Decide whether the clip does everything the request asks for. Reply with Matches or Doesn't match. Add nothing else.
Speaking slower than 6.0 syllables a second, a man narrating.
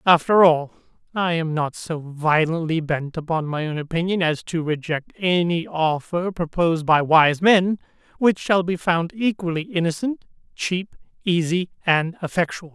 Matches